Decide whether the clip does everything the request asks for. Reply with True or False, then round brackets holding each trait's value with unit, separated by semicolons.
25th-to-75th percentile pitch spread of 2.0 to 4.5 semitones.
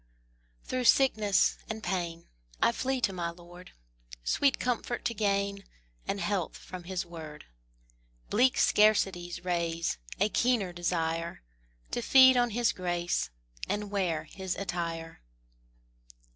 True (4.0 semitones)